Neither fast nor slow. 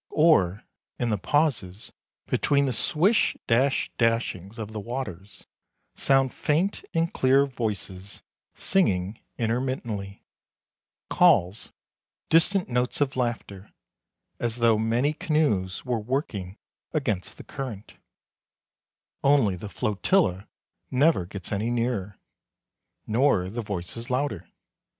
No: slow, 105 wpm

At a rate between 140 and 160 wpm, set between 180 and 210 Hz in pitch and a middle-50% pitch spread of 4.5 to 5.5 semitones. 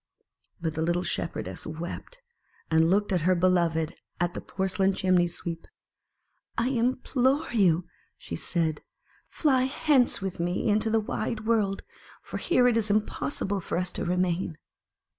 Yes: average, 145 wpm; medium, 185 Hz; average, 4.8 semitones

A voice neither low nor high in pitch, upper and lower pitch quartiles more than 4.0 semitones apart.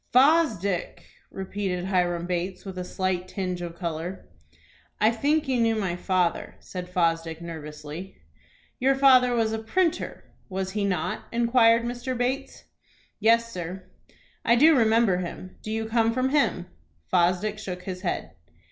No: high, 195 Hz; average, 4.6 semitones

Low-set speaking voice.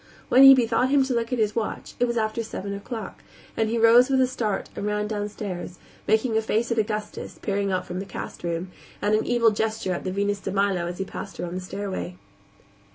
No: high, 210 Hz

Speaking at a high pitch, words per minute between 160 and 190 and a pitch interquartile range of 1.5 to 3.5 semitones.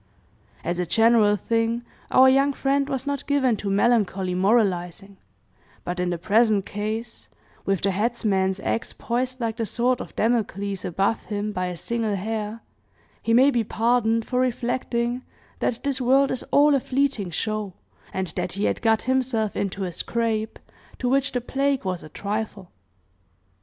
No: high, 225 Hz; average, 165 wpm; average, 4.0 semitones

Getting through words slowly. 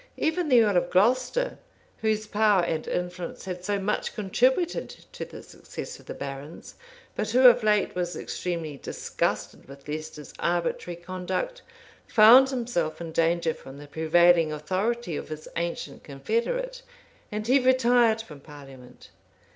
No: average, 145 wpm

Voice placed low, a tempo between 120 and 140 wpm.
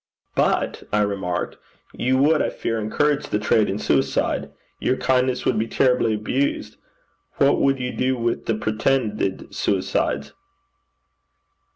Yes: low, 120 Hz; slow, 135 wpm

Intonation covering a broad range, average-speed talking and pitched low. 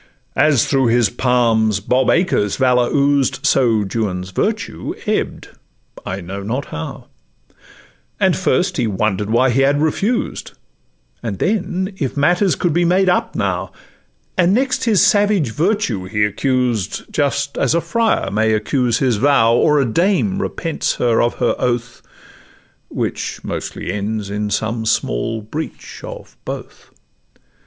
Yes: wide, 7.5 semitones; average, 145 wpm; low, 125 Hz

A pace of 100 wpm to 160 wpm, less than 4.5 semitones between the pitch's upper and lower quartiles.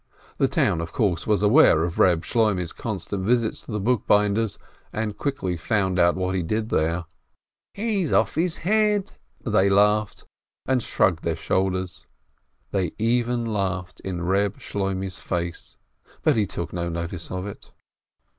Yes: average, 155 wpm; average, 4.0 semitones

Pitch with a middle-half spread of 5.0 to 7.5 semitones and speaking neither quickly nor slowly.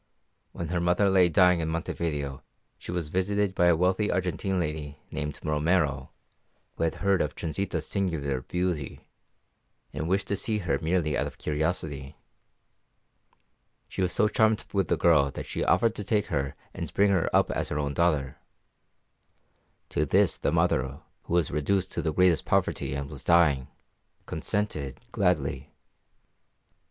No: average, 3.9 semitones; average, 155 wpm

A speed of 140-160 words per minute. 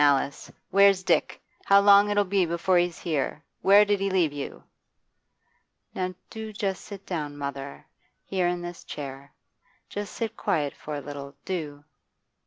Yes: average, 155 wpm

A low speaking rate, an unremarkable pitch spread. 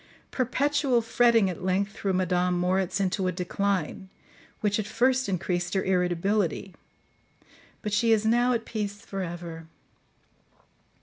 Yes: slow, 130 wpm; average, 3.8 semitones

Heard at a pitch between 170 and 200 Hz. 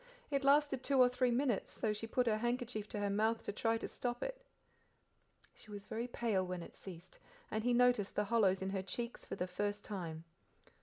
No: high, 220 Hz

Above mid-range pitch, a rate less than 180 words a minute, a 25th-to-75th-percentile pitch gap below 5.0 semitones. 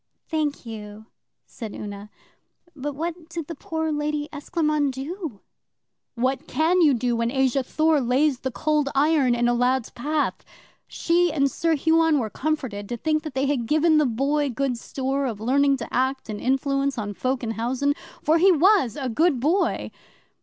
Yes: very high, 275 Hz; average, 170 wpm; average, 4.0 semitones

